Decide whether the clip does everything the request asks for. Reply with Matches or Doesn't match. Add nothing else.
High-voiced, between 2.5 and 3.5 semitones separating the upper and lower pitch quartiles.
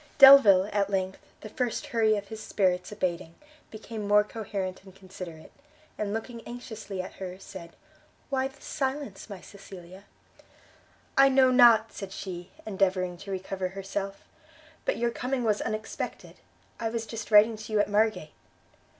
Matches